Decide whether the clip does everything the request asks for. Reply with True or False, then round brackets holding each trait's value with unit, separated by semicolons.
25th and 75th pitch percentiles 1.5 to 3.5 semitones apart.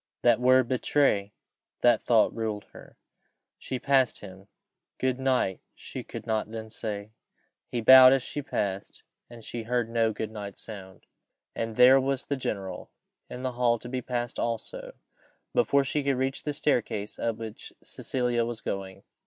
True (3.1 semitones)